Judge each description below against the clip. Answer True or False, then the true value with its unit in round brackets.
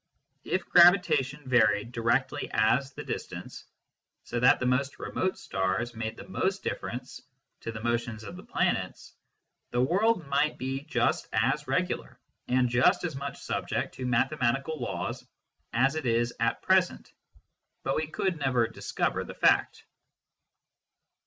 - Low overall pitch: True (130 Hz)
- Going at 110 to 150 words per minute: True (140 wpm)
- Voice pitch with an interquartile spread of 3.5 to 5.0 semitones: True (4.4 semitones)